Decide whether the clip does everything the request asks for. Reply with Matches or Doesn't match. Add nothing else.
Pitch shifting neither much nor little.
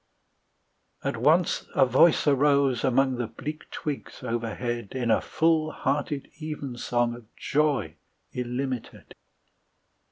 Matches